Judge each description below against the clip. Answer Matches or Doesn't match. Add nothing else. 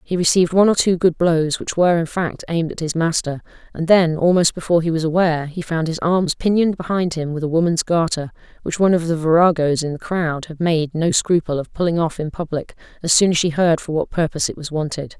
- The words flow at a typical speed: Doesn't match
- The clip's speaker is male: Doesn't match